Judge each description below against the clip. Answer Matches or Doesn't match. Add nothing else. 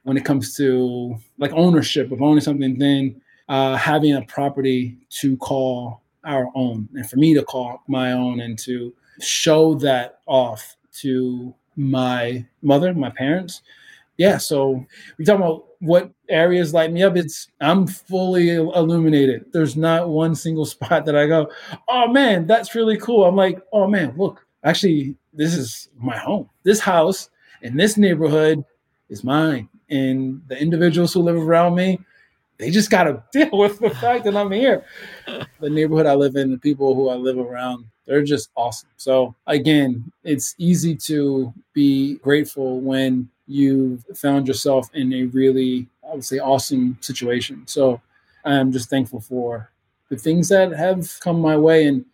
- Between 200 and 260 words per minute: Doesn't match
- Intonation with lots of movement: Doesn't match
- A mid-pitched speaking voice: Matches